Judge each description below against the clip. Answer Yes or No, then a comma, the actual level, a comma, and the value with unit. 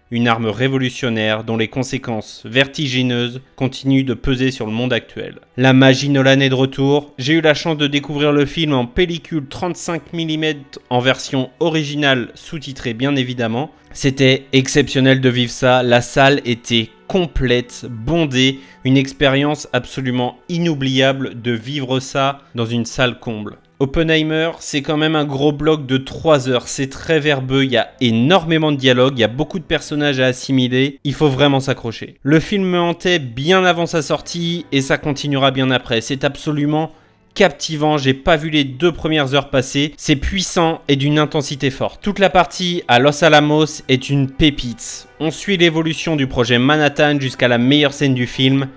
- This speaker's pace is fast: No, average, 175 wpm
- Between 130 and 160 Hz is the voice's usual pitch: Yes, medium, 140 Hz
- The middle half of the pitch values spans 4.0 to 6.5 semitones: No, average, 3.3 semitones